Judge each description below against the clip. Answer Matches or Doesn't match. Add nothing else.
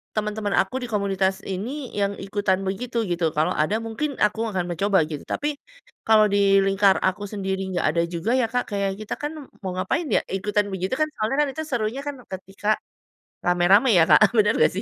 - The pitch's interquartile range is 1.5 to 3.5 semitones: Matches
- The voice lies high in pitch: Matches